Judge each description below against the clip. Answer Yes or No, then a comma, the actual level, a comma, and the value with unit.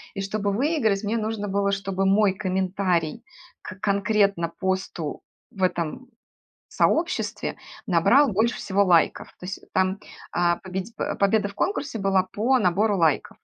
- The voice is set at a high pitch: Yes, high, 195 Hz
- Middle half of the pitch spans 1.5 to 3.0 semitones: Yes, narrow, 2.4 semitones